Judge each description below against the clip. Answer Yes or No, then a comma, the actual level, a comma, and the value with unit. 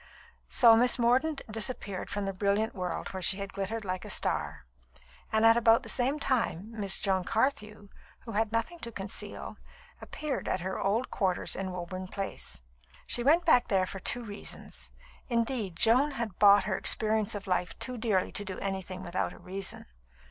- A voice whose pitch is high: Yes, high, 210 Hz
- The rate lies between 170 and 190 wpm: Yes, average, 175 wpm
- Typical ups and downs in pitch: Yes, average, 3.6 semitones